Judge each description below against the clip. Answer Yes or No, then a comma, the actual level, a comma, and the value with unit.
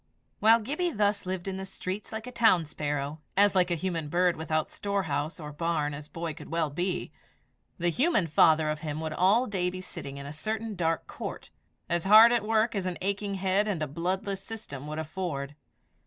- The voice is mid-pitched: Yes, medium, 180 Hz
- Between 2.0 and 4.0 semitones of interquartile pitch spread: No, average, 4.6 semitones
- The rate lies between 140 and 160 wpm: No, average, 200 wpm